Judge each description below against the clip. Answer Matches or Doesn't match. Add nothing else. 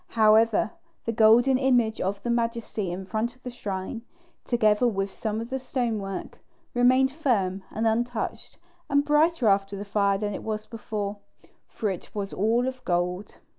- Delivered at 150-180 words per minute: Matches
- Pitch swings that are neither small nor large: Matches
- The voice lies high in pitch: Matches